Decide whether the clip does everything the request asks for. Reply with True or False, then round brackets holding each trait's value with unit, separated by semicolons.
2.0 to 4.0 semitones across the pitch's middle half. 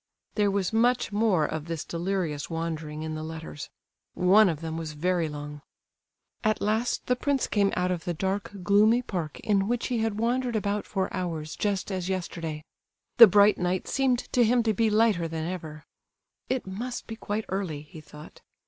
False (5.0 semitones)